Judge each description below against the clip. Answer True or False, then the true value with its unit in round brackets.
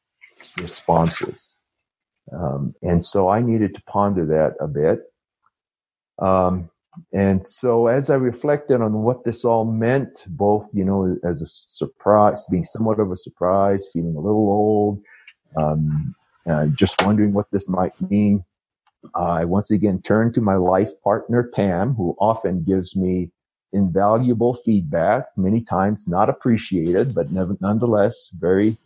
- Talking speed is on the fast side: False (140 wpm)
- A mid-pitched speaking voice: False (100 Hz)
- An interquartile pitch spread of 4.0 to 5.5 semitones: False (3.5 semitones)